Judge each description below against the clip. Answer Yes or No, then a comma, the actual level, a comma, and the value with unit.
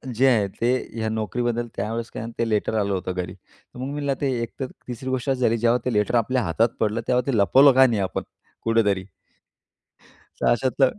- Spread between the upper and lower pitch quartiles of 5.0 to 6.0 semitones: No, average, 3.3 semitones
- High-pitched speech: No, low, 115 Hz